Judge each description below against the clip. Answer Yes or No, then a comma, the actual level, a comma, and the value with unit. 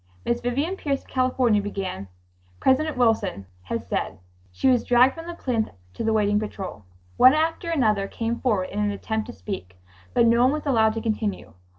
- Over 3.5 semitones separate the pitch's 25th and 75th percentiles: Yes, average, 4.1 semitones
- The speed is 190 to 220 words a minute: Yes, average, 195 wpm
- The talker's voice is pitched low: No, high, 225 Hz